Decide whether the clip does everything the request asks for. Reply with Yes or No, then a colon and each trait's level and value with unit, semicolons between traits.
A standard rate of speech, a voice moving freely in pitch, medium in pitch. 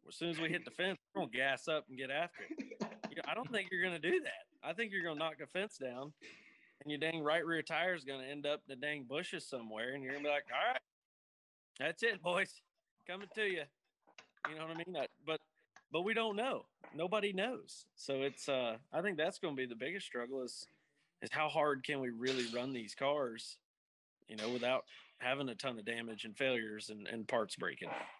No: fast, 230 wpm; wide, 5.8 semitones; medium, 145 Hz